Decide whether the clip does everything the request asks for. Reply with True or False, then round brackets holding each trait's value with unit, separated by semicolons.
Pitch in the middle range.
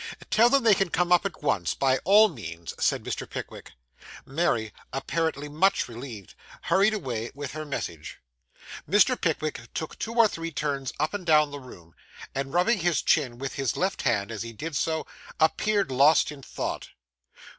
True (150 Hz)